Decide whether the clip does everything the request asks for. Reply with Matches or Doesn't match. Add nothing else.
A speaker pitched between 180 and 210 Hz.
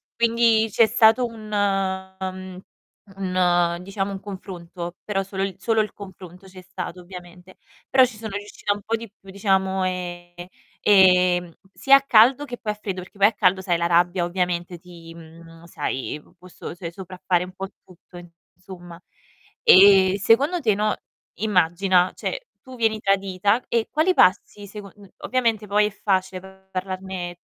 Matches